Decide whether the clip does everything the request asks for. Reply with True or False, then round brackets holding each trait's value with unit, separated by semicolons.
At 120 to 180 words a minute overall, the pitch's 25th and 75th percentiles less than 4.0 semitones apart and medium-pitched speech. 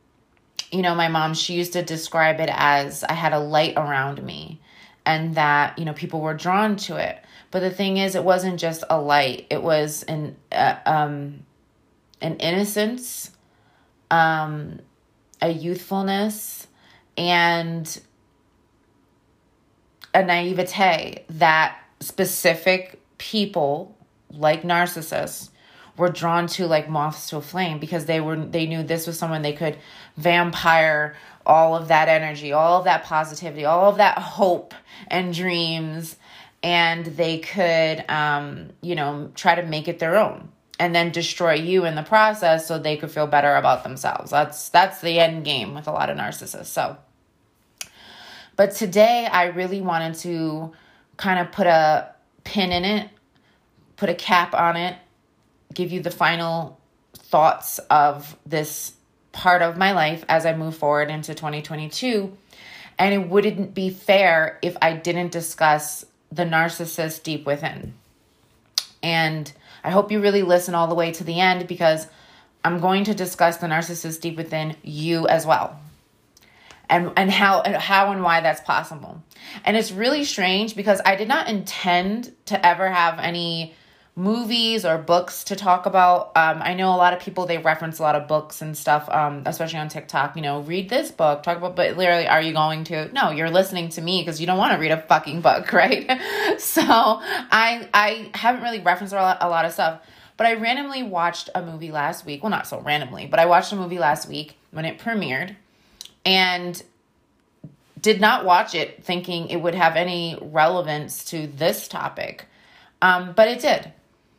True (165 wpm; 2.9 semitones; 170 Hz)